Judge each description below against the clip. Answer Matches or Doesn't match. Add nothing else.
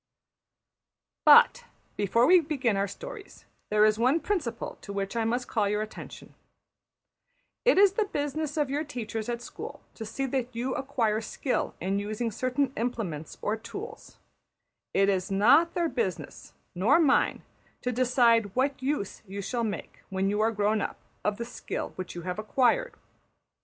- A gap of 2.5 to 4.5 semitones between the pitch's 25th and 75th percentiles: Doesn't match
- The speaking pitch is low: Doesn't match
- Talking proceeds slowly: Doesn't match